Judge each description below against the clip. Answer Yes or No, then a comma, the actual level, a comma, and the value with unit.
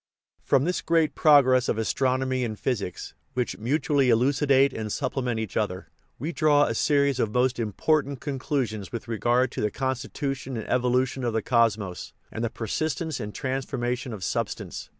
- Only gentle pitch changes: No, average, 3.5 semitones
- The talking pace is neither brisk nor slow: Yes, average, 160 wpm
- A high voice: No, low, 125 Hz